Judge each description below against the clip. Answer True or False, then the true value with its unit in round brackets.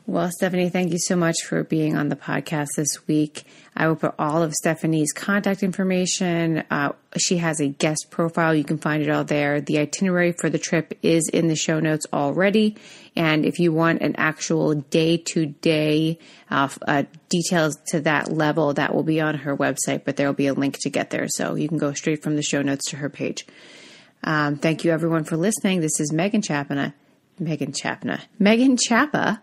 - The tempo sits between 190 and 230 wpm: True (200 wpm)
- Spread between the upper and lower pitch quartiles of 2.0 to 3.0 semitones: True (2.6 semitones)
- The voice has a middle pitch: True (160 Hz)